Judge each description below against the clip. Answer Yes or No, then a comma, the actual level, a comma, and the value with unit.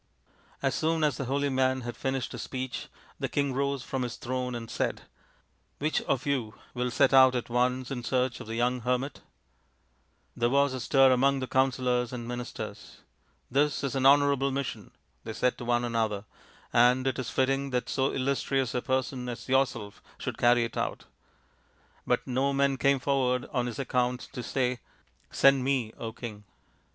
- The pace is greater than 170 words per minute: Yes, average, 190 wpm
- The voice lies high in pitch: No, low, 130 Hz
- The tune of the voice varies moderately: No, narrow, 1.9 semitones